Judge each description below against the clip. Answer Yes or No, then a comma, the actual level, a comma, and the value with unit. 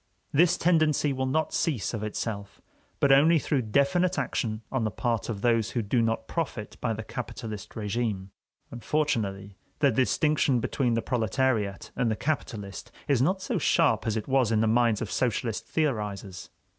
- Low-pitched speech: Yes, low, 120 Hz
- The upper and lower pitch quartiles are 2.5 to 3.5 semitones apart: No, average, 4.4 semitones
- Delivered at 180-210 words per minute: No, average, 170 wpm